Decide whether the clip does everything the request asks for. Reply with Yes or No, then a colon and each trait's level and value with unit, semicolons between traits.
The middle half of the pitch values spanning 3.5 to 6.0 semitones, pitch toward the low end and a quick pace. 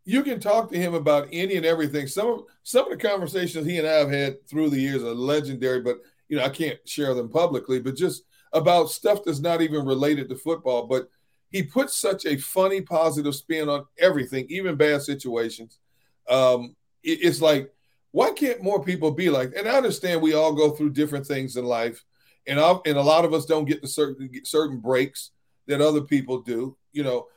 No: average, 4.4 semitones; medium, 150 Hz; fast, 210 wpm